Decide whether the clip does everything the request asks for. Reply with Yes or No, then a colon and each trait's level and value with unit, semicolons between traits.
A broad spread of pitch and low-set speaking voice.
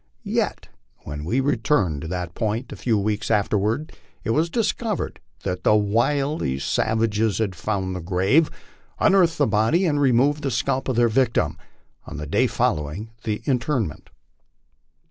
Yes: wide, 5.7 semitones; low, 115 Hz